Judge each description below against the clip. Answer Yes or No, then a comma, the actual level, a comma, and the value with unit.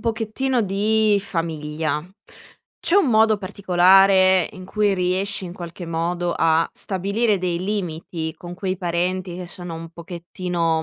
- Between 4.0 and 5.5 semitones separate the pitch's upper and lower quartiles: No, average, 2.8 semitones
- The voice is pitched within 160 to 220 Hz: Yes, medium, 185 Hz